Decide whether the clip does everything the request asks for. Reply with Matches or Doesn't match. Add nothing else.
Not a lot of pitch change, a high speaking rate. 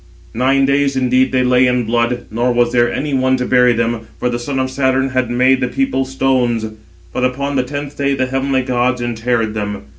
Matches